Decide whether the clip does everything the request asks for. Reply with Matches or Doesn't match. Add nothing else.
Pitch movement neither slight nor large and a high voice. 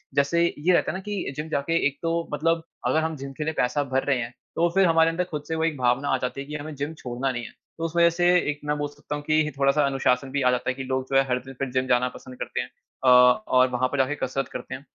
Doesn't match